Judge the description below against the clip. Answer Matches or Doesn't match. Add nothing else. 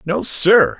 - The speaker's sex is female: Doesn't match